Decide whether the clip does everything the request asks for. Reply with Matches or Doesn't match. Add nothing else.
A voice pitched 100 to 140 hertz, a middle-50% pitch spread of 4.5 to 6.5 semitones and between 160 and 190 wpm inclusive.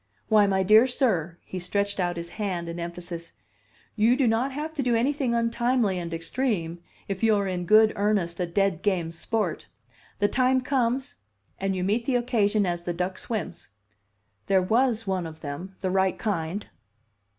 Doesn't match